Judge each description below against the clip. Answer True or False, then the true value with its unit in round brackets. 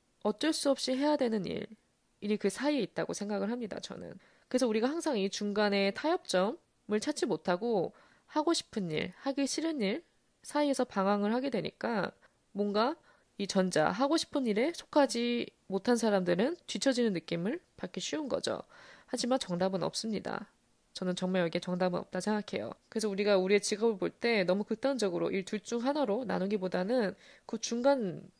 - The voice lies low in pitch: False (220 Hz)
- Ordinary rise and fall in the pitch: True (4.9 semitones)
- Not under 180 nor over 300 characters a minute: False (350 characters per minute)